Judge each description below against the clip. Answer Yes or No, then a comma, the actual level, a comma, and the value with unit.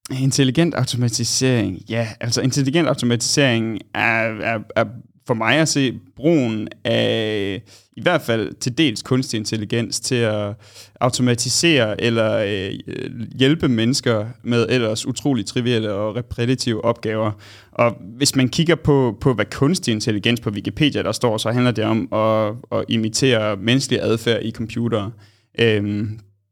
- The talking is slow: Yes, slow, 140 wpm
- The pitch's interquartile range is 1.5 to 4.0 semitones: Yes, average, 2.9 semitones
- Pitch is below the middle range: Yes, low, 115 Hz